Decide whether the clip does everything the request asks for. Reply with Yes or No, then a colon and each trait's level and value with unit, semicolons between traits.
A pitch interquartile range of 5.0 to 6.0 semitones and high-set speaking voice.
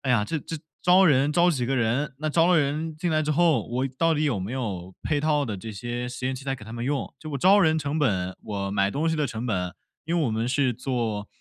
No: wide, 5.4 semitones; low, 135 Hz